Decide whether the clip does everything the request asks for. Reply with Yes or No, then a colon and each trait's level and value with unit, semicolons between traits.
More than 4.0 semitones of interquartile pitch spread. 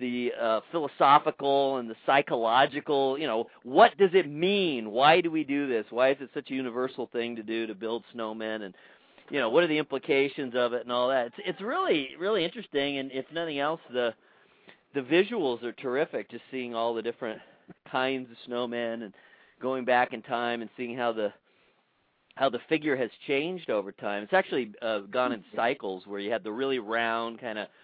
No: average, 3.4 semitones